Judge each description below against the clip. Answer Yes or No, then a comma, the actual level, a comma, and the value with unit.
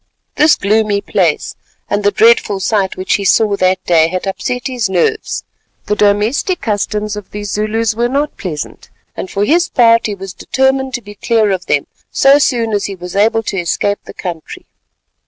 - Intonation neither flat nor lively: Yes, average, 3.1 semitones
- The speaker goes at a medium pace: Yes, average, 185 wpm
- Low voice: No, high, 210 Hz